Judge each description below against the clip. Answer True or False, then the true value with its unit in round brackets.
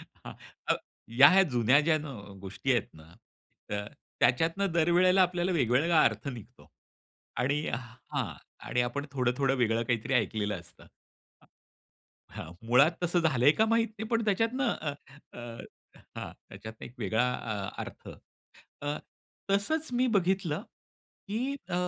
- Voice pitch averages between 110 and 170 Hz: True (140 Hz)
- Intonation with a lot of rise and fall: True (7.5 semitones)